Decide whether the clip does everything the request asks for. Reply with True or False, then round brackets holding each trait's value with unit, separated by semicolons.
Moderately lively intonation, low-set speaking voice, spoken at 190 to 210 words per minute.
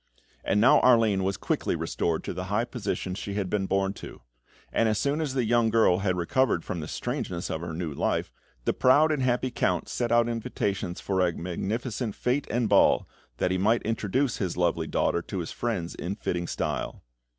True (4.6 semitones; 105 Hz; 200 wpm)